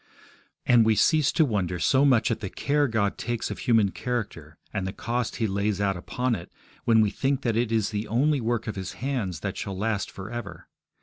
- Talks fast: Yes, fast, 220 wpm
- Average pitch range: Yes, average, 3.7 semitones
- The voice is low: Yes, low, 110 Hz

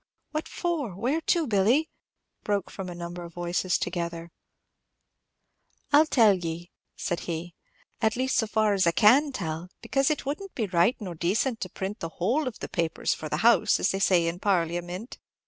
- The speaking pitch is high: Yes, high, 195 Hz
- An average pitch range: No, wide, 6.2 semitones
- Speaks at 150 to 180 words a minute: No, average, 190 wpm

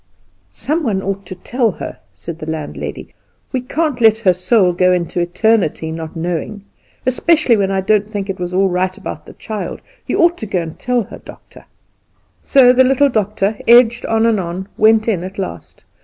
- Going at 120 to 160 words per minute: No, average, 195 wpm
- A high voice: Yes, high, 205 Hz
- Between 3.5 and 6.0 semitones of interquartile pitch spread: Yes, average, 4.5 semitones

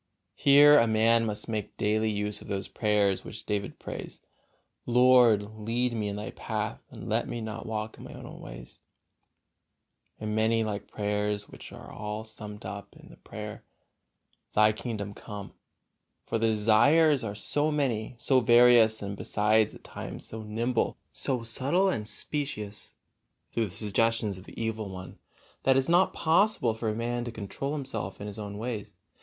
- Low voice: Yes, low, 110 Hz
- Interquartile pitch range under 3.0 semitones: Yes, narrow, 2.6 semitones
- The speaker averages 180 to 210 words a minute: No, average, 170 wpm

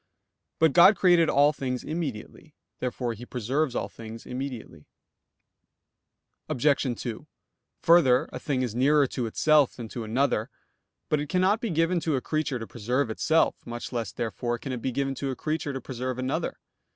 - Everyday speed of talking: Yes, average, 170 wpm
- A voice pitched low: Yes, low, 130 Hz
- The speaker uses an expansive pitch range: No, average, 4.2 semitones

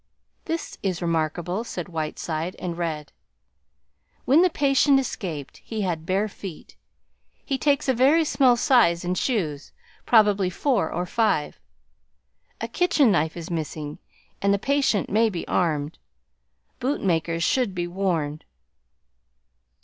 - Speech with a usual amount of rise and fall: No, wide, 6.9 semitones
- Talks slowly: Yes, slow, 130 wpm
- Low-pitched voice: No, medium, 185 Hz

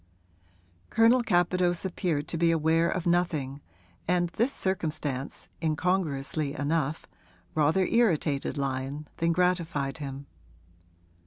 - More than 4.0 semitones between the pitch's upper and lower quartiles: No, average, 3.7 semitones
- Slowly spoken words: Yes, slow, 100 wpm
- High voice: No, medium, 165 Hz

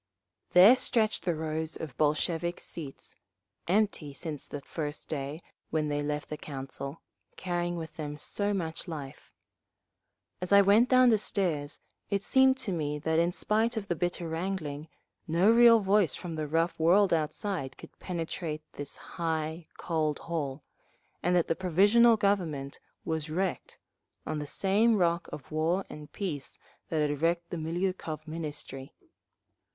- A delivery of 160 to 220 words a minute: No, average, 145 wpm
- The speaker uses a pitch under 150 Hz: No, medium, 165 Hz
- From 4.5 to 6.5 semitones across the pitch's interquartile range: No, average, 4.0 semitones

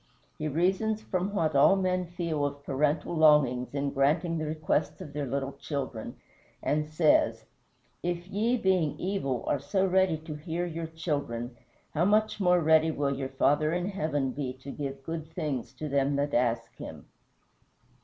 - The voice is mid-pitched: Yes, medium, 155 Hz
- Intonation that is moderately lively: Yes, average, 3.9 semitones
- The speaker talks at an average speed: Yes, average, 165 wpm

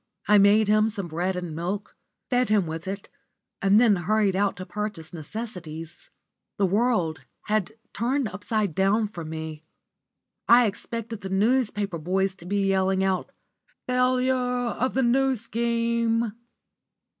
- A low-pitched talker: No, high, 205 Hz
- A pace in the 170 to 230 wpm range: No, average, 140 wpm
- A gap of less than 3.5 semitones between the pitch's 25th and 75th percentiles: No, average, 4.0 semitones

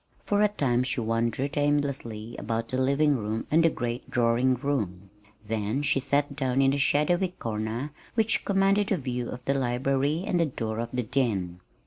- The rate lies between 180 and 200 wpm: Yes, average, 185 wpm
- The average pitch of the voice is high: No, low, 130 Hz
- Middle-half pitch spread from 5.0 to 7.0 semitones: No, average, 3.8 semitones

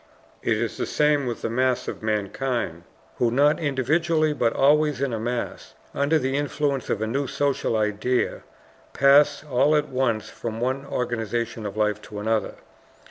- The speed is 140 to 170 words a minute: Yes, average, 165 wpm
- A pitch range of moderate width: Yes, average, 4.1 semitones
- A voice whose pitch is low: Yes, low, 130 Hz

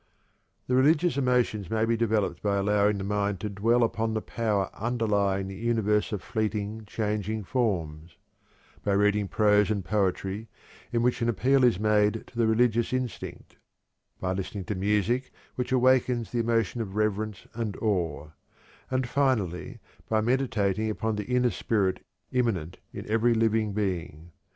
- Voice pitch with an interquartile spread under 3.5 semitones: Yes, average, 2.8 semitones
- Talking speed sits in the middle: Yes, average, 155 wpm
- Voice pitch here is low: Yes, low, 110 Hz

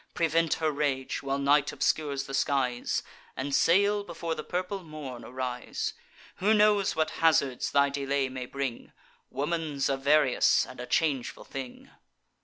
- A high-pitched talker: No, medium, 140 Hz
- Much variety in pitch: No, average, 3.4 semitones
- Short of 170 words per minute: Yes, average, 145 wpm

